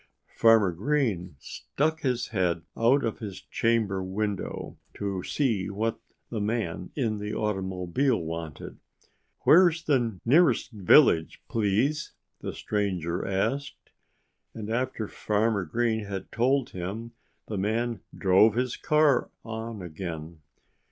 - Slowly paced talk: Yes, slow, 120 wpm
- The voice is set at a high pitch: No, low, 110 Hz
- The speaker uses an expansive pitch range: No, average, 4.2 semitones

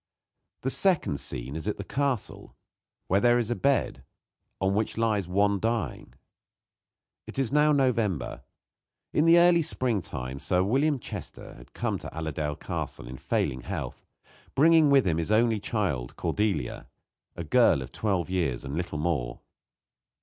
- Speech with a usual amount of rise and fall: No, wide, 8.7 semitones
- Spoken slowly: No, average, 150 wpm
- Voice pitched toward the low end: Yes, low, 105 Hz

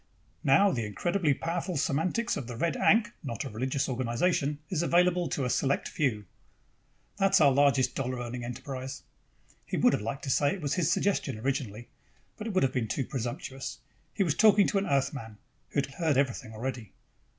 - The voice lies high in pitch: No, low, 135 Hz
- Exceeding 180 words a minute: Yes, average, 190 wpm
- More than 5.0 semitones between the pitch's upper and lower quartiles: Yes, wide, 5.6 semitones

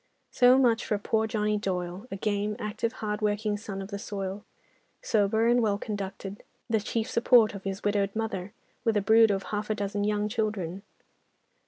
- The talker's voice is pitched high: Yes, high, 210 Hz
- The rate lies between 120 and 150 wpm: No, average, 175 wpm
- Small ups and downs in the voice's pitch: Yes, narrow, 1.7 semitones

